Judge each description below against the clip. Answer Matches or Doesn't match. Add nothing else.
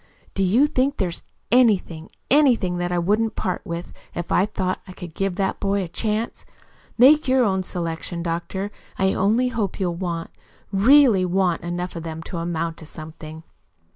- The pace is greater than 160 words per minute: Matches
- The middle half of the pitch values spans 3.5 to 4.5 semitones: Matches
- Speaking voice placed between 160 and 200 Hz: Matches